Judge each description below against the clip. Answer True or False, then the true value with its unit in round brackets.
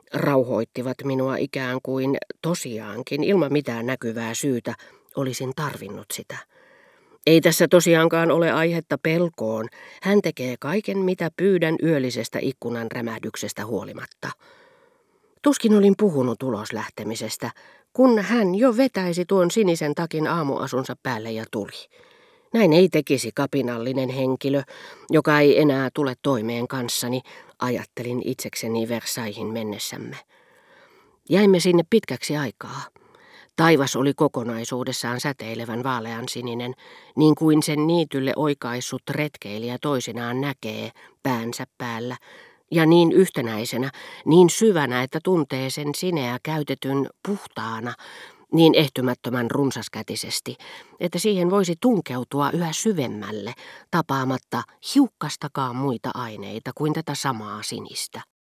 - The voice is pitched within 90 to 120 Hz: False (140 Hz)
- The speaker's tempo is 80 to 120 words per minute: True (110 wpm)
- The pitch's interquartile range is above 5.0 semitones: True (5.4 semitones)